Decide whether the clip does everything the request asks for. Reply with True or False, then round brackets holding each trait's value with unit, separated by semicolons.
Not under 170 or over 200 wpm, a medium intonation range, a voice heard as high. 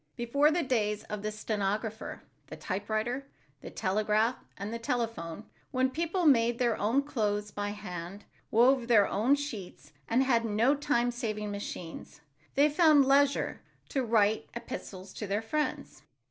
False (145 wpm; 4.2 semitones; 225 Hz)